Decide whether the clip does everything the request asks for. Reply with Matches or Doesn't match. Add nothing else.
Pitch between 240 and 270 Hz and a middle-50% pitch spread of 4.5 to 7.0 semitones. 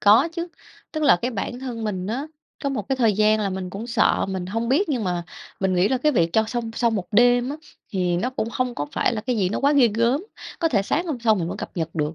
Doesn't match